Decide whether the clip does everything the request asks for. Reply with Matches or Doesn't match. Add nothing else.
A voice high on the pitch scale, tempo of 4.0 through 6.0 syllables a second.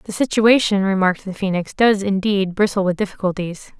Matches